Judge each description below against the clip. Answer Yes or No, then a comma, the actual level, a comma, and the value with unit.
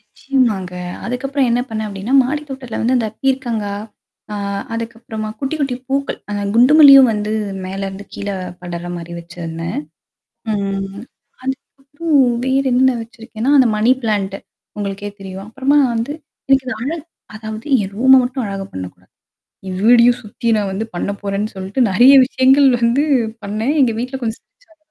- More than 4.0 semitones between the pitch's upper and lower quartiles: Yes, average, 4.7 semitones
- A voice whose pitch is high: Yes, high, 230 Hz